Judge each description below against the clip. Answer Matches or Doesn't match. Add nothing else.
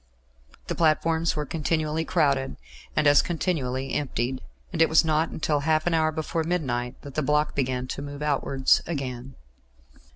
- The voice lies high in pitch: Doesn't match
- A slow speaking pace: Doesn't match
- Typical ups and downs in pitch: Matches